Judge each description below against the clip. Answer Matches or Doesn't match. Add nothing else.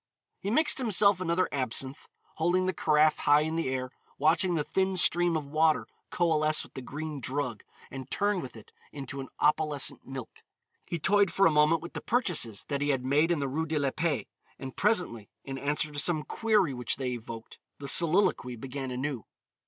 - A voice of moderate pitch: Matches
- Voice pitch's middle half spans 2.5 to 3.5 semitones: Doesn't match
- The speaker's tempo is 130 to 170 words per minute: Doesn't match